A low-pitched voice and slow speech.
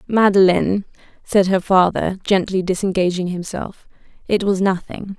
No: high, 190 Hz; slow, 115 wpm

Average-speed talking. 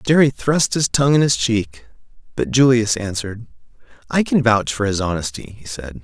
Yes: average, 180 wpm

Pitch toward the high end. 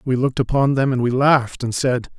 No: low, 130 Hz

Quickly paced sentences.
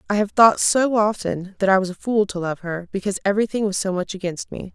Yes: fast, 255 wpm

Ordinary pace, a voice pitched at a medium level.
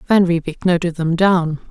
Yes: average, 175 wpm; medium, 170 Hz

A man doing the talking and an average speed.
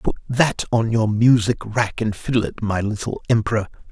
Yes: male; average, 185 wpm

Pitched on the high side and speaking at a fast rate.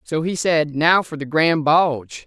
No: medium, 155 Hz; fast, 210 wpm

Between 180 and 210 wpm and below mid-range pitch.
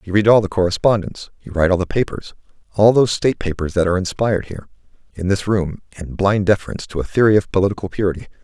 Yes: fast, 205 wpm; very low, 95 Hz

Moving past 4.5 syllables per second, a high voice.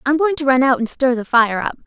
Yes: 5.9 syllables/s; very high, 265 Hz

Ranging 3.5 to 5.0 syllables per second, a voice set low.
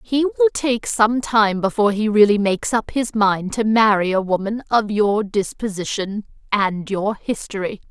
No: 4.6 syllables/s; high, 210 Hz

